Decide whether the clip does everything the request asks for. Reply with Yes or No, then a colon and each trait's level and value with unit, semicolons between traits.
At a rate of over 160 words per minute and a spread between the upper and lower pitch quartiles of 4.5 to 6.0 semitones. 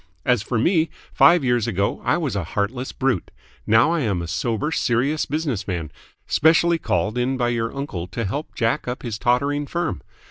Yes: average, 185 wpm; wide, 5.5 semitones